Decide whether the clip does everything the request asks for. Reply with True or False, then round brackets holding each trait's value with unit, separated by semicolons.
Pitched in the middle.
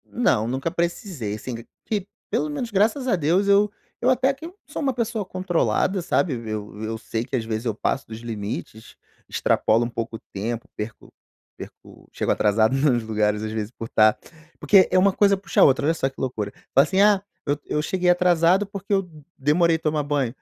True (150 Hz)